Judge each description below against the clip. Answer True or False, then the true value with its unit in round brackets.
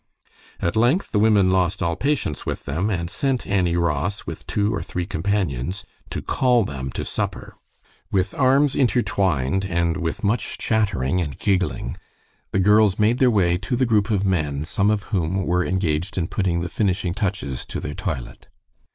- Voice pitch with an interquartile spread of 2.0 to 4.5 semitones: True (3.9 semitones)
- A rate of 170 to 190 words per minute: True (175 wpm)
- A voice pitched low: True (95 Hz)